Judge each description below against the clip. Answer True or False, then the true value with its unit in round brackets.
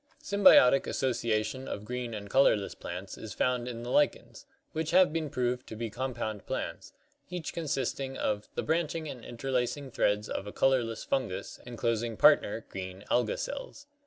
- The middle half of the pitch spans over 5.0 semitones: False (4.1 semitones)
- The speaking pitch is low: True (125 Hz)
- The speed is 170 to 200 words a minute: False (160 wpm)